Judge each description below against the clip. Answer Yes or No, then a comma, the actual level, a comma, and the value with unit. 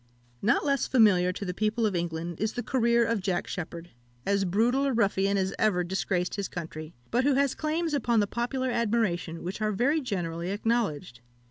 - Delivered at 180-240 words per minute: Yes, average, 190 wpm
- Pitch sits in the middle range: No, high, 205 Hz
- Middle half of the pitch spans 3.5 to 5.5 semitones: Yes, average, 5.0 semitones